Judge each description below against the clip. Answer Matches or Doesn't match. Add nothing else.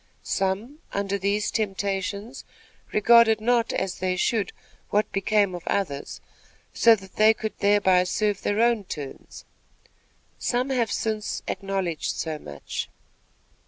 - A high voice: Matches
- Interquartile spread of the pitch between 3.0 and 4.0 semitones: Doesn't match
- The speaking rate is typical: Doesn't match